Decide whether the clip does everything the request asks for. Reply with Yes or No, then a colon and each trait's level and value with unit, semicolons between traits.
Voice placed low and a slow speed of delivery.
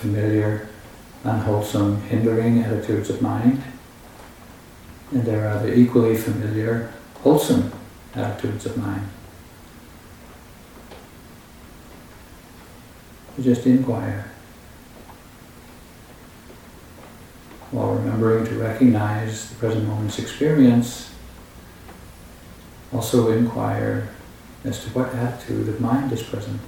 Yes: low, 115 Hz; slow, 85 wpm